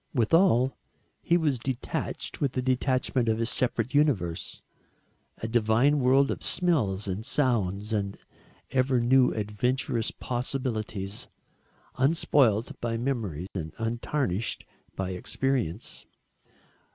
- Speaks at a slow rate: Yes, slow, 105 wpm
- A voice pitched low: Yes, low, 120 Hz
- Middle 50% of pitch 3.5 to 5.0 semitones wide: Yes, average, 3.9 semitones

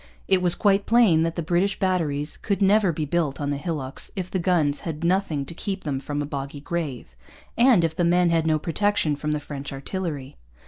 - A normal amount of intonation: Yes, average, 4.2 semitones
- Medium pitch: Yes, medium, 165 Hz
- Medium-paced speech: No, fast, 215 wpm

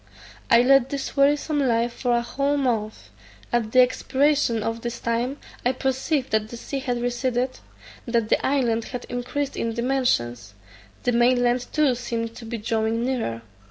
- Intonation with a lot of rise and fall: No, narrow, 2.4 semitones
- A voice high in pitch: Yes, high, 245 Hz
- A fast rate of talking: No, average, 165 wpm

